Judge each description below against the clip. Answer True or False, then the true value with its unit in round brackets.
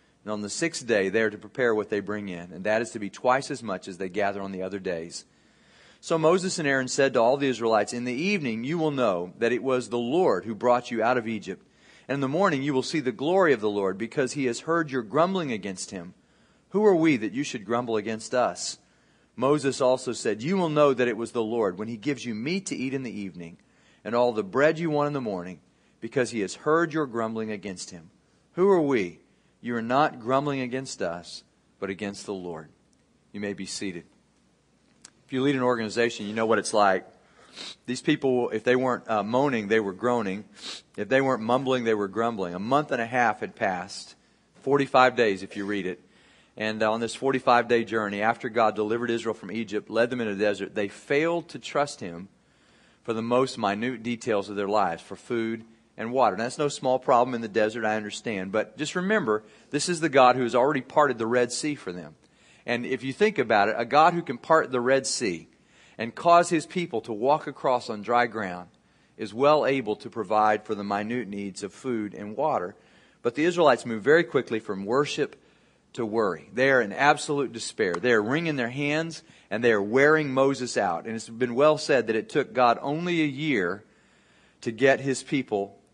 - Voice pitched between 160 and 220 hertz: False (120 Hz)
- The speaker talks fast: True (220 wpm)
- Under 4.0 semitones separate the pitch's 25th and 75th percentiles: False (4.4 semitones)